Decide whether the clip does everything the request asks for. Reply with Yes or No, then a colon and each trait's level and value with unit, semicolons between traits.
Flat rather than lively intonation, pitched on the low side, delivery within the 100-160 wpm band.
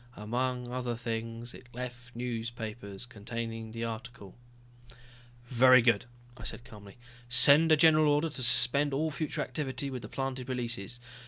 Yes: narrow, 2.2 semitones; low, 120 Hz; average, 145 wpm